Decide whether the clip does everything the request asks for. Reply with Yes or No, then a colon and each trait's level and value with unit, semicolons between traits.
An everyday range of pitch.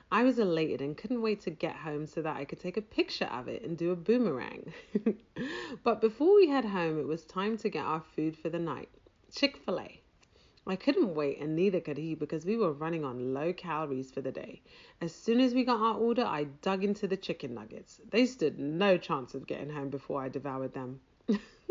No: wide, 6.4 semitones